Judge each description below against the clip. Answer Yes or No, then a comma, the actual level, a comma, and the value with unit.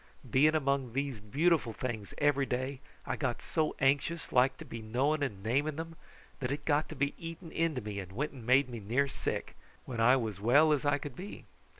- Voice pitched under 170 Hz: Yes, low, 135 Hz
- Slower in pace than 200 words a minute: No, fast, 205 wpm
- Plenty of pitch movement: No, average, 3.8 semitones